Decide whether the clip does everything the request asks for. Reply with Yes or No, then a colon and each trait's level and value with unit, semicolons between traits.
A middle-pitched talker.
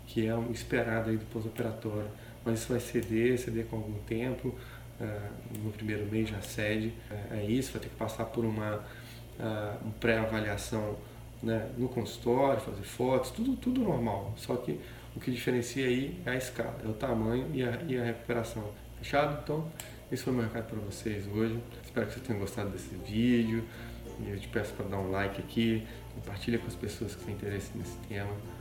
No: low, 115 Hz